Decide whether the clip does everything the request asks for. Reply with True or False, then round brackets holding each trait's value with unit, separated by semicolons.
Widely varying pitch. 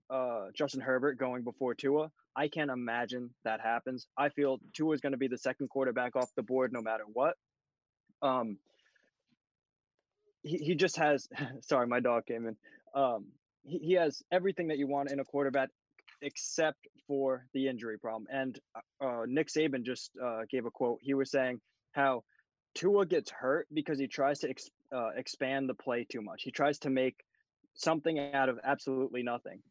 False (2.8 semitones)